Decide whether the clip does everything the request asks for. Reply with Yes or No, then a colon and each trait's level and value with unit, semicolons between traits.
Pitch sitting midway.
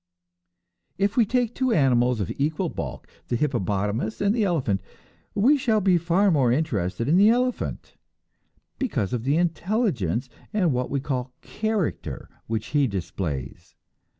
Yes: medium, 150 Hz